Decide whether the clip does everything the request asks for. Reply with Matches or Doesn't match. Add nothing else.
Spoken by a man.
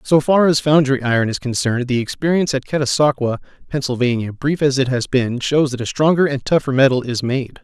Matches